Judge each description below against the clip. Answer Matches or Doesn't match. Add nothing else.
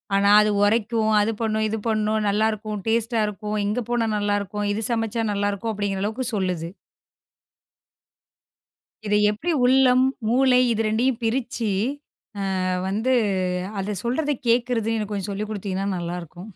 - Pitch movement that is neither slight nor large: Doesn't match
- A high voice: Matches